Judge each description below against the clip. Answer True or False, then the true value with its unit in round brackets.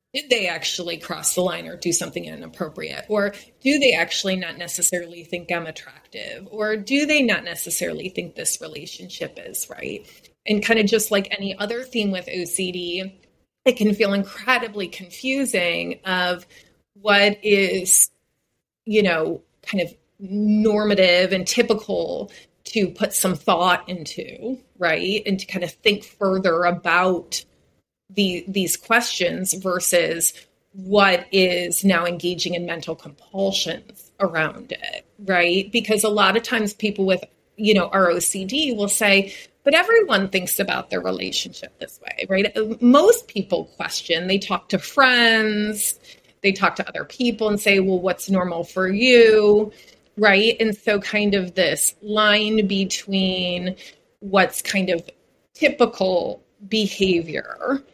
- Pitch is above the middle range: True (195 Hz)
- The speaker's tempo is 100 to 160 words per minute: True (140 wpm)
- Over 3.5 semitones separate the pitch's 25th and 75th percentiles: False (3.1 semitones)